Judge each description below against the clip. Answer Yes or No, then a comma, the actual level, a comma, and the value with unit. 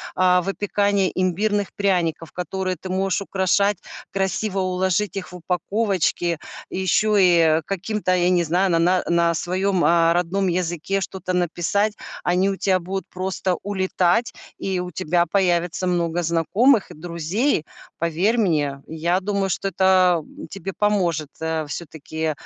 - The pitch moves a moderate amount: No, narrow, 2.3 semitones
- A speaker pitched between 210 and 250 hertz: No, medium, 185 Hz